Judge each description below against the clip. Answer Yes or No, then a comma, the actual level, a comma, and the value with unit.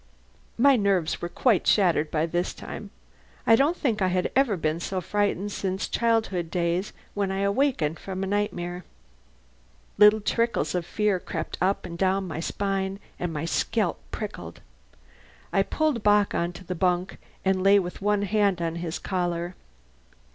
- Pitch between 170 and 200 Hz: Yes, high, 190 Hz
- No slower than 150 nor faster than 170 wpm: Yes, average, 155 wpm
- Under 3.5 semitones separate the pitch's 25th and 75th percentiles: Yes, average, 2.9 semitones